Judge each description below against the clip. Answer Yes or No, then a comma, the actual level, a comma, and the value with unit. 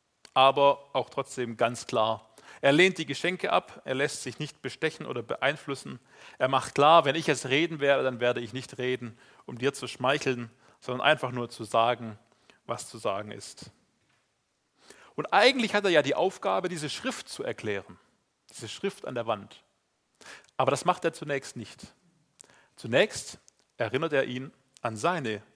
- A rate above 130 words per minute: Yes, average, 165 wpm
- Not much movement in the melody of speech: No, average, 3.7 semitones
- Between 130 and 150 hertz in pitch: Yes, low, 135 Hz